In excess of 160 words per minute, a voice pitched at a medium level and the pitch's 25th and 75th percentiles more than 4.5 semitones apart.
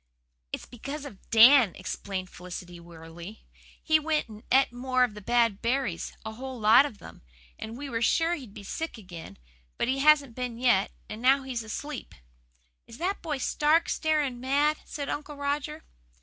No: average, 175 wpm; very high, 250 Hz; average, 5.0 semitones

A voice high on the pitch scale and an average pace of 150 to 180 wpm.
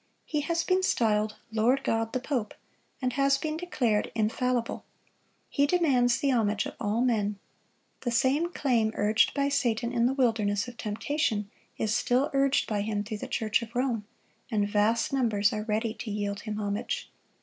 Yes: high, 230 Hz; average, 170 wpm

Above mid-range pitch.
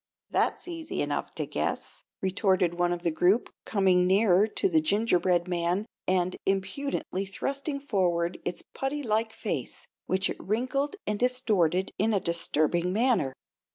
Yes: high, 195 Hz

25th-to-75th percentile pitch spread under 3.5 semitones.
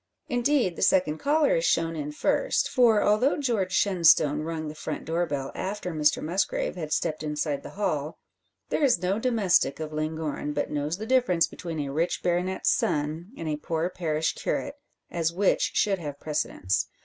No: average, 5.0 semitones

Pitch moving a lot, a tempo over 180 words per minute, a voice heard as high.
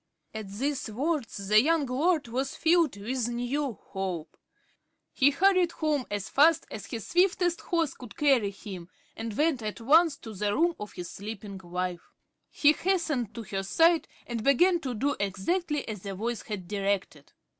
No: wide, 7.3 semitones; average, 165 wpm; high, 240 Hz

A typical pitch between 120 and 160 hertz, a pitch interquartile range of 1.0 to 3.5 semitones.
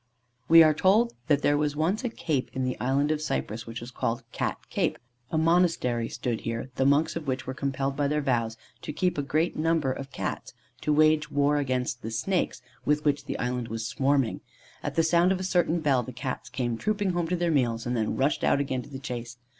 No: medium, 140 Hz; average, 4.2 semitones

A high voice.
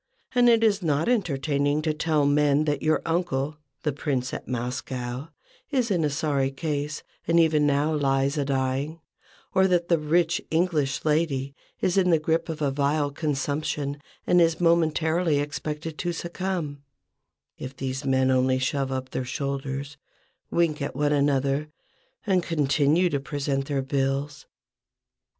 No: medium, 150 Hz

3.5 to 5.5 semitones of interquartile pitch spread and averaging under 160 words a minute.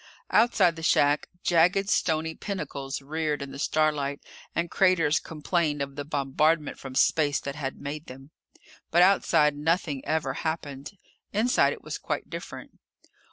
No: average, 2.8 semitones; average, 145 wpm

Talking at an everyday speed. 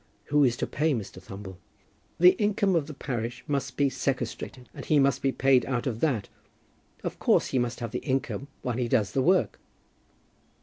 Yes: average, 190 wpm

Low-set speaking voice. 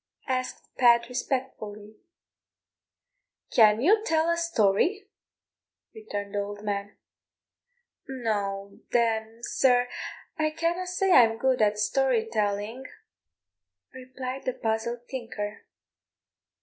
No: high, 235 Hz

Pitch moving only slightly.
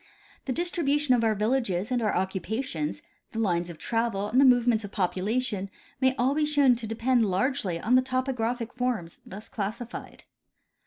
No: average, 4.3 semitones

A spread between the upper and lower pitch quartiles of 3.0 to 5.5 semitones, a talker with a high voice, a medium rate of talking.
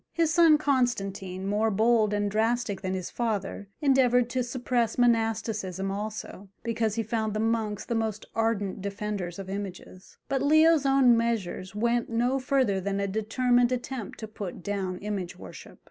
Yes: average, 3.5 semitones; high, 220 Hz; average, 160 wpm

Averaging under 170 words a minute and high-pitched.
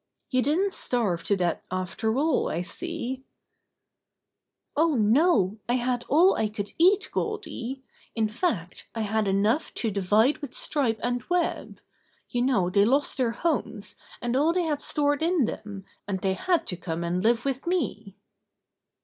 Yes: average, 160 wpm; high, 240 Hz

